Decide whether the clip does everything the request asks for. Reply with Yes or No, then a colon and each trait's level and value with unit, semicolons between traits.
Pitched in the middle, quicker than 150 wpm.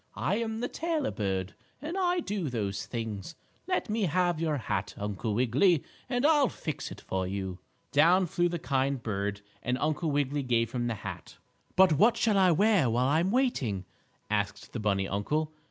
Yes: medium, 145 Hz; average, 180 wpm